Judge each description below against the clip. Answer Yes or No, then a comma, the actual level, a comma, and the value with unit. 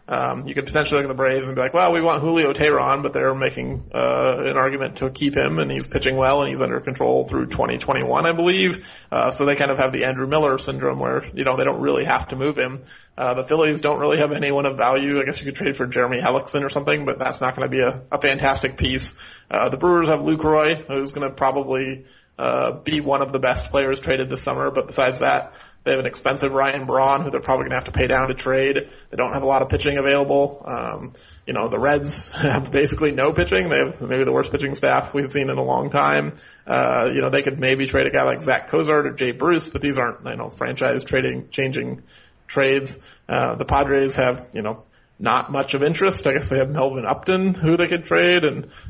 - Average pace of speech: No, fast, 245 wpm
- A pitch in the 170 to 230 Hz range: No, low, 135 Hz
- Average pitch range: No, narrow, 2.0 semitones